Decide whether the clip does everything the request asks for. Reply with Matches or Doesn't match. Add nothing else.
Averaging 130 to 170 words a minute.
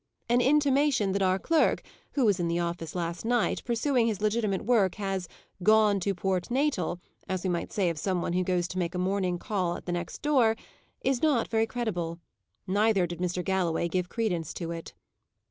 Doesn't match